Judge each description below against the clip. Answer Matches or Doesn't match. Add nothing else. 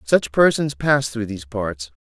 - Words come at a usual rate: Matches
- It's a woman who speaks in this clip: Doesn't match